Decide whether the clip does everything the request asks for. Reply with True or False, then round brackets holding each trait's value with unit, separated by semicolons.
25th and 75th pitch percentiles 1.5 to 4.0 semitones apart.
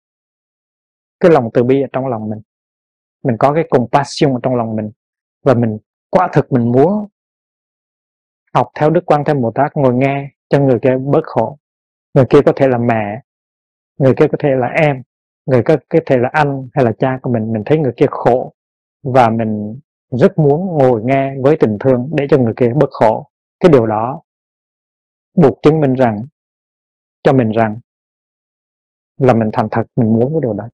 True (3.7 semitones)